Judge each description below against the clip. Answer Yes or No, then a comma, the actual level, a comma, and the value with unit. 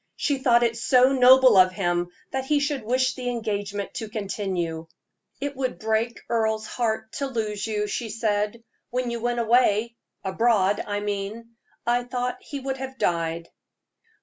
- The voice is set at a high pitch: Yes, high, 230 Hz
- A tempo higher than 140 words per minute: Yes, average, 160 wpm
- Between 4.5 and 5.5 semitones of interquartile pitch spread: No, average, 3.4 semitones